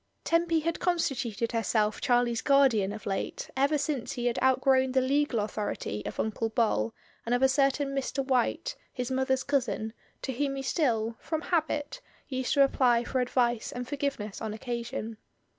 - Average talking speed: Yes, average, 165 wpm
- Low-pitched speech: No, very high, 255 Hz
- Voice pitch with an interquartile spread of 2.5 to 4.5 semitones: Yes, average, 3.2 semitones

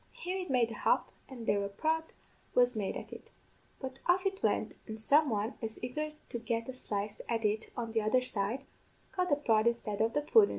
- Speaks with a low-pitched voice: No, high, 235 Hz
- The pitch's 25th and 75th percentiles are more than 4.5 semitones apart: Yes, average, 5.2 semitones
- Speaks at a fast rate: Yes, fast, 220 wpm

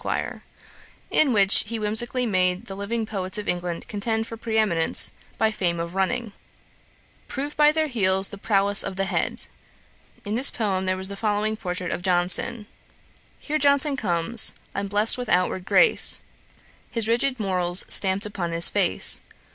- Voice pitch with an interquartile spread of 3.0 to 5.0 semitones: Yes, average, 3.6 semitones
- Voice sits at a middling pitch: No, high, 205 Hz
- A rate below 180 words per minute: Yes, average, 160 wpm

